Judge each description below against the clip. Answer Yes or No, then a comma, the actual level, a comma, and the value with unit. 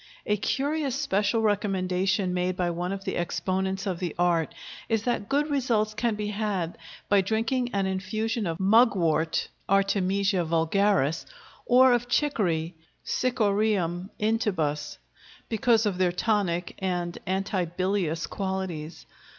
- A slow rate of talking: Yes, slow, 125 wpm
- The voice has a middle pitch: No, high, 195 Hz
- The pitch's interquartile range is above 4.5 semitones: No, average, 3.5 semitones